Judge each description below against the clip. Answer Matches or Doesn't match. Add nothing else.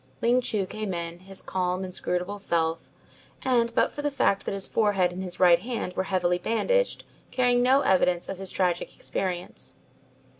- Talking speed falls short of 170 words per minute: Doesn't match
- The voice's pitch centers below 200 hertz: Matches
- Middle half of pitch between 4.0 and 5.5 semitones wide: Matches